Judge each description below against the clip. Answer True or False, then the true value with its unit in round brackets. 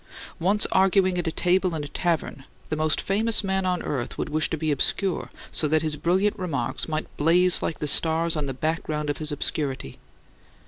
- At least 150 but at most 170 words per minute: False (195 wpm)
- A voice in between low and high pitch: True (160 Hz)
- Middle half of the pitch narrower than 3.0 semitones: False (3.4 semitones)